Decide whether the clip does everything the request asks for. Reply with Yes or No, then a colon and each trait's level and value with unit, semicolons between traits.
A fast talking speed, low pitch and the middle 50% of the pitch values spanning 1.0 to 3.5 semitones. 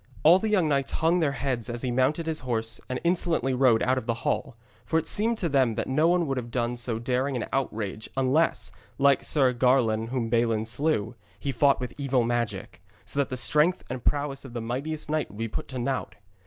No: fast, 220 wpm; low, 130 Hz; average, 3.9 semitones